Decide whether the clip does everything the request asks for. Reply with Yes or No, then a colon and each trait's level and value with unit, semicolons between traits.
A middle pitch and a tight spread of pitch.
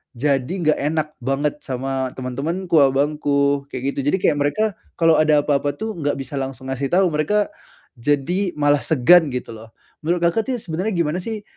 No: medium, 150 Hz; average, 4.0 semitones